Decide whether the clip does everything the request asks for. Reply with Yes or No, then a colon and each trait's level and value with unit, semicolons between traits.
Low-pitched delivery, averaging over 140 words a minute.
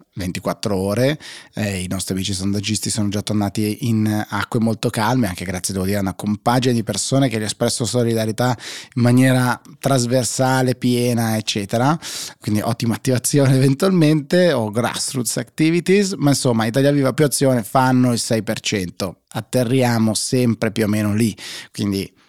Yes: low, 115 Hz; average, 150 wpm